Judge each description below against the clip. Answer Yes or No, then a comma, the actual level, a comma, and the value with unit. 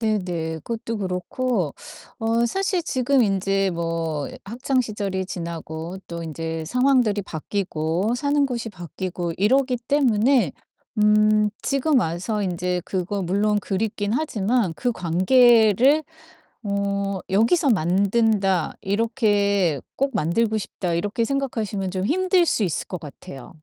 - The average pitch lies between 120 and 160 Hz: No, high, 205 Hz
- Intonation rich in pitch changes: No, average, 4.8 semitones